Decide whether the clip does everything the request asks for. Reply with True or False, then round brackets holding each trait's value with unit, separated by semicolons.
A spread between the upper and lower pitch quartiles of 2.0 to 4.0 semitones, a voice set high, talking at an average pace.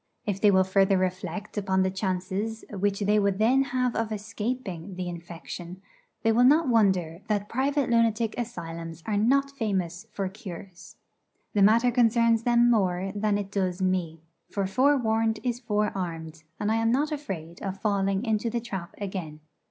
True (3.6 semitones; 205 Hz; 165 wpm)